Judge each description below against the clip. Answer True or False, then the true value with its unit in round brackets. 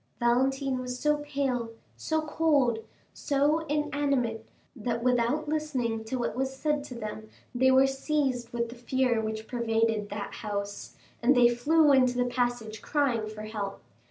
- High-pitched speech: True (245 Hz)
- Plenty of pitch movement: False (3.5 semitones)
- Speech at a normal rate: True (155 wpm)